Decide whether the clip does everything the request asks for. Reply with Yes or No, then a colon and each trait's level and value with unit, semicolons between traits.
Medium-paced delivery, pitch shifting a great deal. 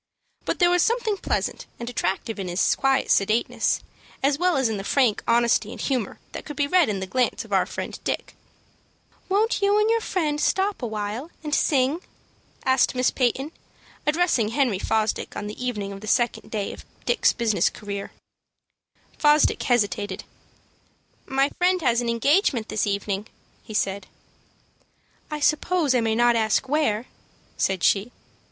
Yes: average, 165 wpm; wide, 5.9 semitones